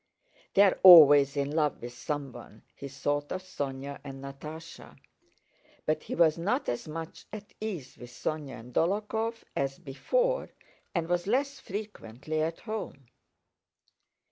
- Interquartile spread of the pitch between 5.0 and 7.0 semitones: Yes, wide, 5.5 semitones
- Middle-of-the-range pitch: Yes, medium, 155 Hz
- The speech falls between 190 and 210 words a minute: No, slow, 135 wpm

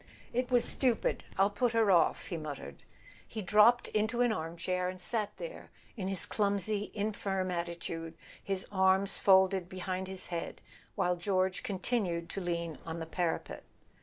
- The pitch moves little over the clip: No, average, 3.2 semitones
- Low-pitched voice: No, high, 190 Hz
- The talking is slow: No, average, 150 wpm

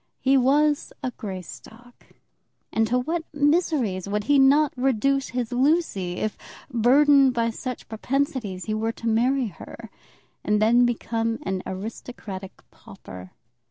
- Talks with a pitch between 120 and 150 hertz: No, high, 240 Hz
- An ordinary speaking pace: No, slow, 130 wpm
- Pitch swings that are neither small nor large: Yes, average, 4.2 semitones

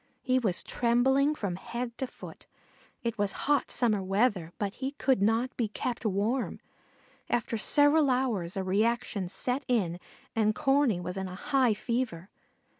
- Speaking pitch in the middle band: No, high, 235 Hz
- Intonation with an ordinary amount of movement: Yes, average, 4.6 semitones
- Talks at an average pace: Yes, average, 155 wpm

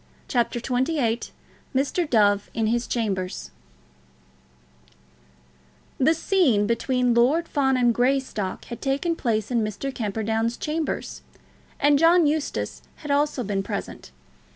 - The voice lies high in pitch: Yes, high, 245 Hz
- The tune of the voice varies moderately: Yes, average, 4.5 semitones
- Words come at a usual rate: No, slow, 115 wpm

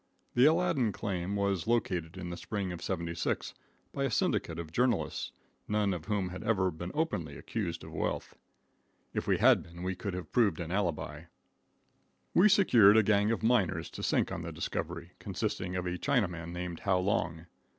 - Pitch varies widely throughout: No, average, 3.9 semitones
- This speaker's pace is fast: No, average, 180 wpm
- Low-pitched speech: Yes, very low, 95 Hz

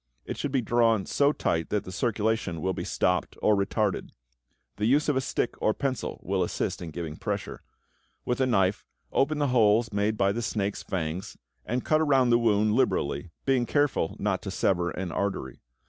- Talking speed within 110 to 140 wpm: No, average, 190 wpm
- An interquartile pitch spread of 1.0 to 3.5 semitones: No, average, 5.0 semitones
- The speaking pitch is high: No, low, 110 Hz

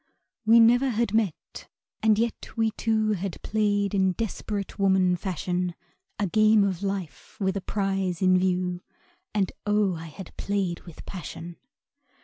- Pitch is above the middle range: Yes, high, 195 Hz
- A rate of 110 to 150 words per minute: Yes, average, 140 wpm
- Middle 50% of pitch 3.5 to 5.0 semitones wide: No, average, 2.8 semitones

